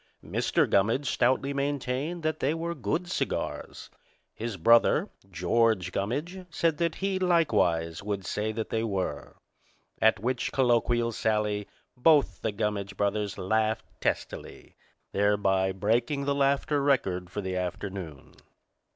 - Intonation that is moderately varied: No, wide, 6.0 semitones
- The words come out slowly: Yes, slow, 125 wpm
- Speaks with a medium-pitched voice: No, low, 115 Hz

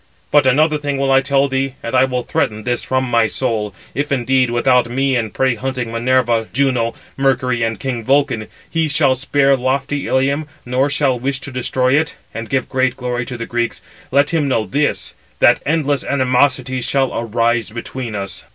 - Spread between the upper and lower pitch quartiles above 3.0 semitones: No, narrow, 2.5 semitones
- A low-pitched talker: Yes, low, 130 Hz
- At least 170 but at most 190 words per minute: Yes, average, 185 wpm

